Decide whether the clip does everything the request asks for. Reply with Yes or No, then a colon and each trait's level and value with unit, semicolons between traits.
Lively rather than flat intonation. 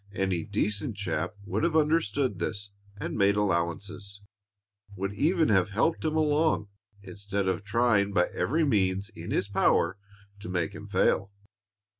No: average, 3.5 semitones